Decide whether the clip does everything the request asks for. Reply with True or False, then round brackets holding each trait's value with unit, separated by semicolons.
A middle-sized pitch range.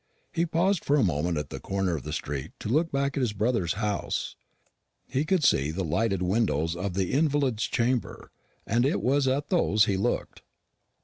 False (7.3 semitones)